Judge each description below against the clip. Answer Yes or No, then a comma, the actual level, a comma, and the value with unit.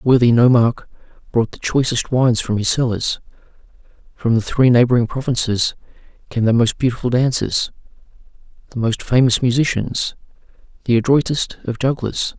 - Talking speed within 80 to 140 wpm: Yes, slow, 135 wpm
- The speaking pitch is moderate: No, low, 120 Hz